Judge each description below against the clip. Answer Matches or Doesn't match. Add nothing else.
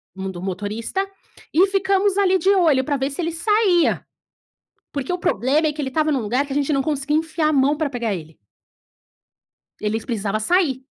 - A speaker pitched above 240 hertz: Matches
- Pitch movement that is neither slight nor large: Doesn't match